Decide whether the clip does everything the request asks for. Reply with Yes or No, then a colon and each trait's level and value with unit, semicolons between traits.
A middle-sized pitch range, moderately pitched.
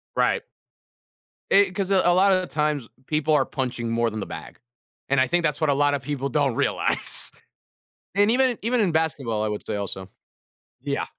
No: wide, 6.6 semitones; medium, 150 Hz